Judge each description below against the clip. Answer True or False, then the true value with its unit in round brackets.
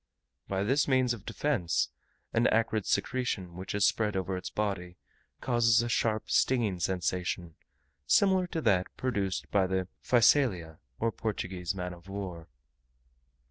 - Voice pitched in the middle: False (100 Hz)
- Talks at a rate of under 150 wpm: True (140 wpm)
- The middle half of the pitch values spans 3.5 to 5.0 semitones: True (4.5 semitones)